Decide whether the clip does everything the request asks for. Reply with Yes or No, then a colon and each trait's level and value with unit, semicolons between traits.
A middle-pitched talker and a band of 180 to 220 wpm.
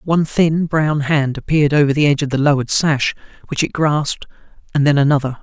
Yes: medium, 145 Hz; average, 190 wpm